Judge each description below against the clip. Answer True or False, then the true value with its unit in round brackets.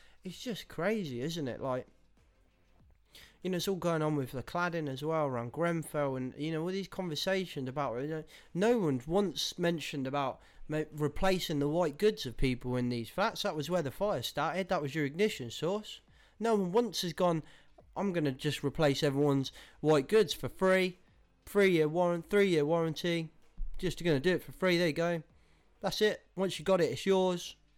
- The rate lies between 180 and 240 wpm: True (190 wpm)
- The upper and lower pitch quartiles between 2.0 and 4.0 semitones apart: False (4.7 semitones)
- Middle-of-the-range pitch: True (160 Hz)